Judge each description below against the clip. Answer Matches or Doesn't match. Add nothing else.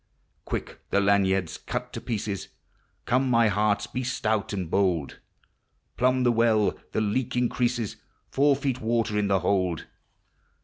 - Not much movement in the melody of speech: Doesn't match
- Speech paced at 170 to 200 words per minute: Doesn't match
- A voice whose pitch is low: Matches